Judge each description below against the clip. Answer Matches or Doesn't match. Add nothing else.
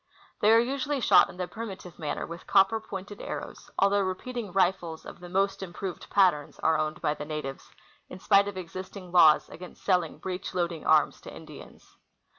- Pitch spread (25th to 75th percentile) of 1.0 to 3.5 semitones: Matches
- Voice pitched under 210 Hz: Matches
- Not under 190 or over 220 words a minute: Doesn't match